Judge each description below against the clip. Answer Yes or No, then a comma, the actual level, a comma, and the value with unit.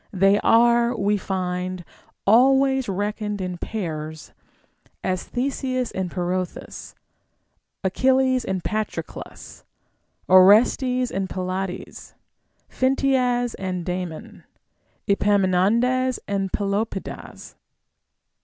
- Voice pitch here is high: Yes, high, 200 Hz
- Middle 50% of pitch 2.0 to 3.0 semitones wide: No, average, 5.0 semitones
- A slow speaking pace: Yes, slow, 80 wpm